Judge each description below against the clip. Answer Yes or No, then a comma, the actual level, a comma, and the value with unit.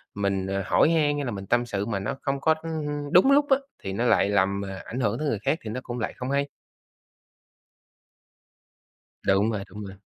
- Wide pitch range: Yes, wide, 6.0 semitones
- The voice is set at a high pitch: No, low, 115 Hz